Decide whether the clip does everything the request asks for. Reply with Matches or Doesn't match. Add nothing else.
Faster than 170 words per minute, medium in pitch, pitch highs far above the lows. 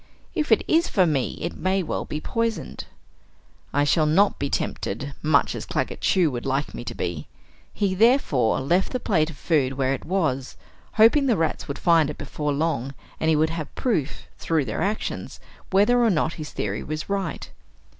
Matches